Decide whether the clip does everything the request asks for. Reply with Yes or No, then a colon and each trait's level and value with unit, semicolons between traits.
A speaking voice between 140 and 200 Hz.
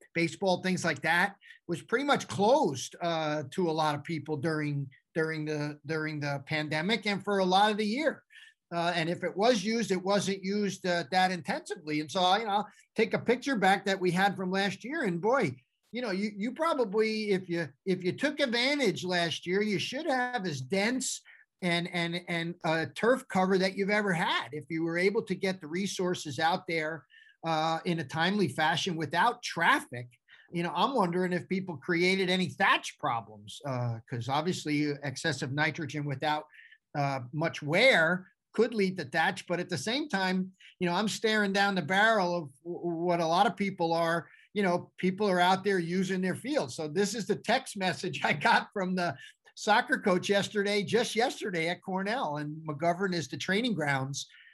Yes: medium, 185 Hz